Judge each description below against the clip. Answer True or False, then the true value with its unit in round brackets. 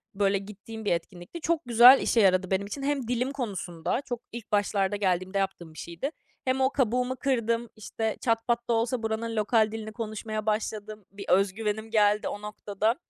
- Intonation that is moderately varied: True (3.0 semitones)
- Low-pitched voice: False (220 Hz)